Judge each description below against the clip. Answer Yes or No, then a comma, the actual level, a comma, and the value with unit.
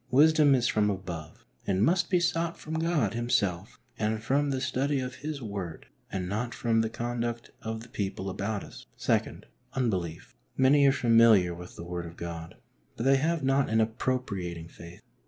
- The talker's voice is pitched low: Yes, low, 115 Hz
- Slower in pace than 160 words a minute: No, average, 175 wpm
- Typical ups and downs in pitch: No, wide, 6.0 semitones